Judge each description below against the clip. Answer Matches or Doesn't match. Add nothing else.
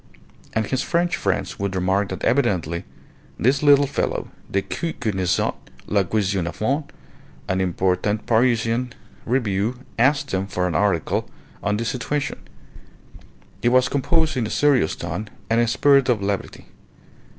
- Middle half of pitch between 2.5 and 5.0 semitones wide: Doesn't match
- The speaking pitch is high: Doesn't match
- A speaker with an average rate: Matches